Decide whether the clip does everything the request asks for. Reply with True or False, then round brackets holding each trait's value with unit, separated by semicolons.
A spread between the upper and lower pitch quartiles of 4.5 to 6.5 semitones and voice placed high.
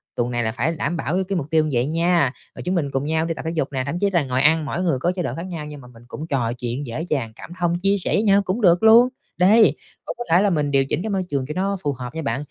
False (5.0 semitones; 160 Hz)